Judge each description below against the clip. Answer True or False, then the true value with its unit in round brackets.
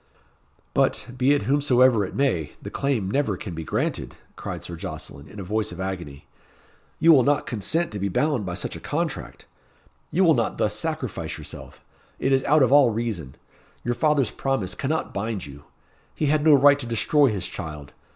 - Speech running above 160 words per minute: True (190 wpm)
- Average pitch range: False (7.1 semitones)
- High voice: False (120 Hz)